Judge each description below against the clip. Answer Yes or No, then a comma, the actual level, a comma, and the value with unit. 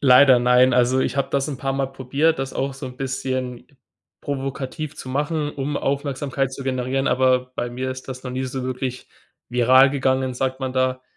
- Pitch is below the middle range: Yes, low, 130 Hz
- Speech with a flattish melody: Yes, narrow, 1.2 semitones